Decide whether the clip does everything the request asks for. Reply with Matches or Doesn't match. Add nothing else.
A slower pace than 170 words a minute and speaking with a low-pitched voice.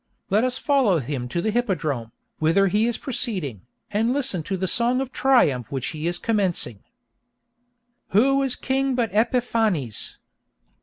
Doesn't match